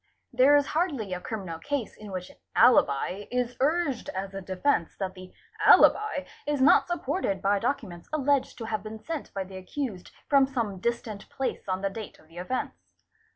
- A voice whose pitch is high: Yes, high, 220 Hz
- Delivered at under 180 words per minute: No, average, 185 wpm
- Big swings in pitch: Yes, wide, 6.5 semitones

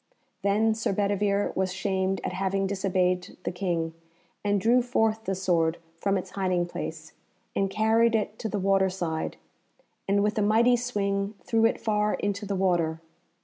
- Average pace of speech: Yes, average, 165 wpm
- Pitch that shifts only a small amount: Yes, narrow, 2.3 semitones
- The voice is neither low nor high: No, high, 195 Hz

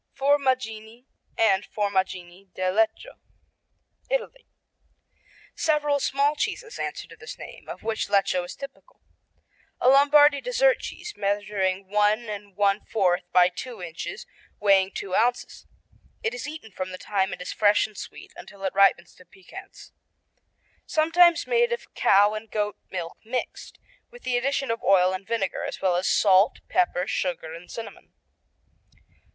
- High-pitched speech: Yes, high, 210 Hz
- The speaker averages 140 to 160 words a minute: Yes, average, 145 wpm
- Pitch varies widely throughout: Yes, wide, 6.7 semitones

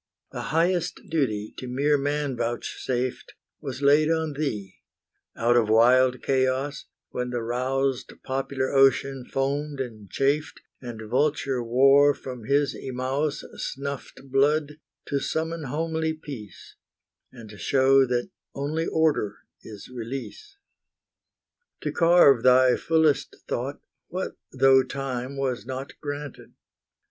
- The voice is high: No, low, 135 Hz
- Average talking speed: No, slow, 115 wpm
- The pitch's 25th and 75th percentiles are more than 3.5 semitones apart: No, average, 2.7 semitones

